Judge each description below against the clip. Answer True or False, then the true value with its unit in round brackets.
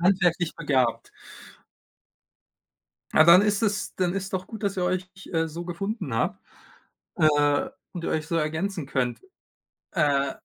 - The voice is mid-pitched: True (170 Hz)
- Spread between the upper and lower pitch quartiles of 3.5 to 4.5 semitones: True (4.2 semitones)